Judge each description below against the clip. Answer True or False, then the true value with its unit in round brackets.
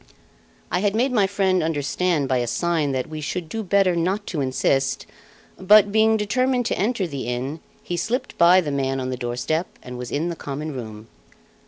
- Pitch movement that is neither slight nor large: False (6.8 semitones)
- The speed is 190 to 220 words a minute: True (195 wpm)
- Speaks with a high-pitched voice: False (165 Hz)